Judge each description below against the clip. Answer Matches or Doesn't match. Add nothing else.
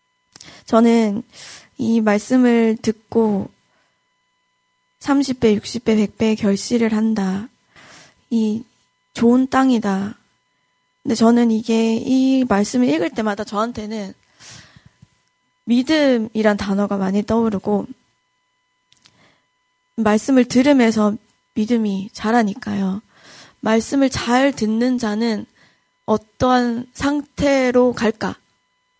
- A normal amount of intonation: Matches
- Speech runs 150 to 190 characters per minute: Matches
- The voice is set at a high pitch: Matches